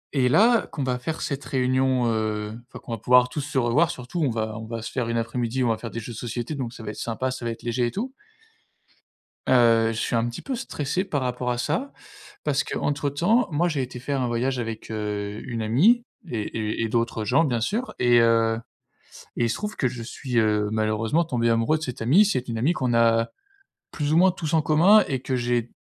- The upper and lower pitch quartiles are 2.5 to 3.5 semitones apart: No, average, 4.2 semitones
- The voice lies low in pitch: Yes, low, 125 Hz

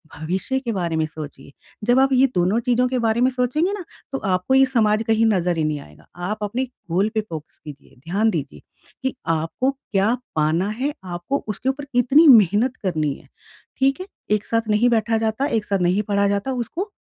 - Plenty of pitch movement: Yes, wide, 6.0 semitones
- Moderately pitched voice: No, high, 215 Hz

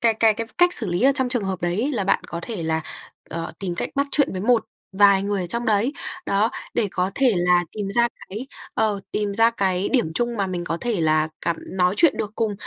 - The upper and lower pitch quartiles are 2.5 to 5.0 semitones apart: Yes, average, 4.5 semitones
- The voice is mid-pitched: No, high, 205 Hz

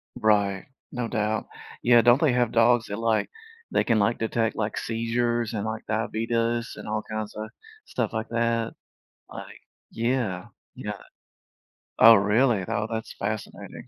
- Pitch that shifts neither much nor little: No, narrow, 1.5 semitones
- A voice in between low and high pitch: No, low, 115 Hz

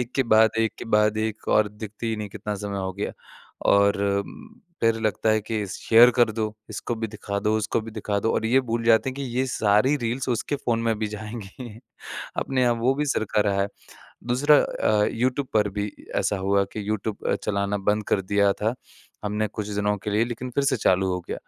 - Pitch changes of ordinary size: No, narrow, 2.2 semitones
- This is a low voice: Yes, low, 110 Hz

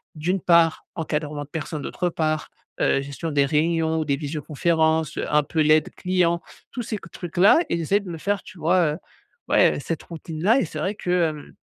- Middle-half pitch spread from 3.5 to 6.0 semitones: No, narrow, 2.6 semitones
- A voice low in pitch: No, medium, 160 Hz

